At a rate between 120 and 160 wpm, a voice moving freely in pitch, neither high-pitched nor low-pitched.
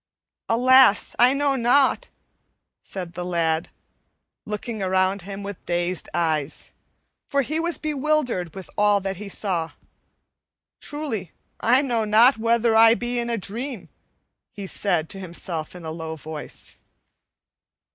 No: slow, 135 wpm; wide, 5.7 semitones; high, 210 Hz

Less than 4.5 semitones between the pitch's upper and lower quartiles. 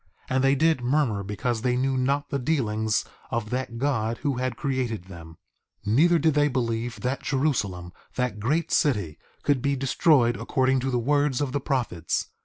Yes: average, 3.8 semitones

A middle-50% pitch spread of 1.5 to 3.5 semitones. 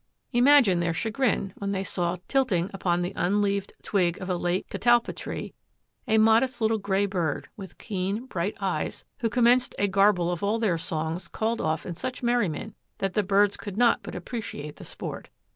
No: average, 4.2 semitones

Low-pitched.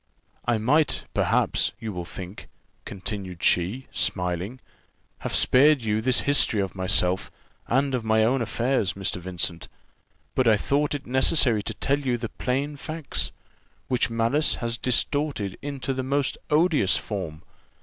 Yes: low, 120 Hz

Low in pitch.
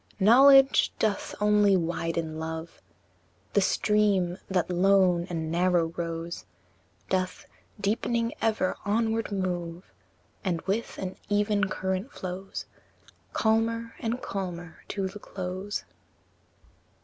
No: high, 190 Hz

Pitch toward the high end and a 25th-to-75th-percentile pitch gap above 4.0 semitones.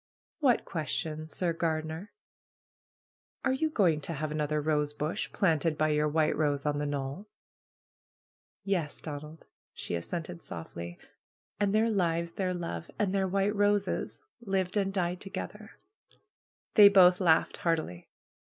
No: medium, 165 Hz; average, 4.4 semitones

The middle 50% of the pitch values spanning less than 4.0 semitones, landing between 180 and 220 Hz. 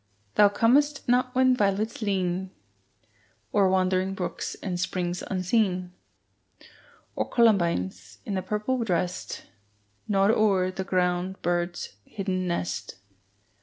Yes: average, 2.9 semitones; high, 190 Hz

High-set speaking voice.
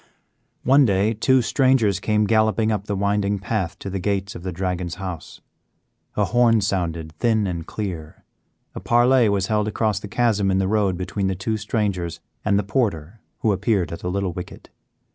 No: low, 100 Hz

